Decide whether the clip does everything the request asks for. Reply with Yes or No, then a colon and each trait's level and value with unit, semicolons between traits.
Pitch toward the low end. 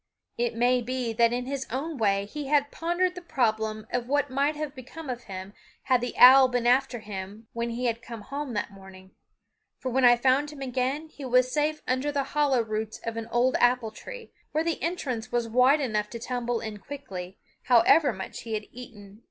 No: high, 245 Hz